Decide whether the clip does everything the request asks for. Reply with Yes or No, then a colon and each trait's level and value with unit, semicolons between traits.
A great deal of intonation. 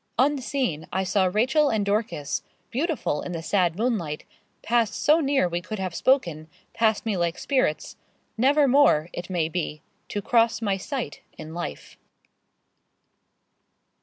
Yes: wide, 6.9 semitones